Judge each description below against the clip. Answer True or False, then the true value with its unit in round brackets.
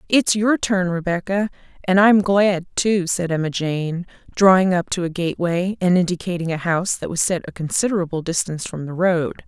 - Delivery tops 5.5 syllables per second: False (5.3 syllables/s)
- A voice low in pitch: False (180 Hz)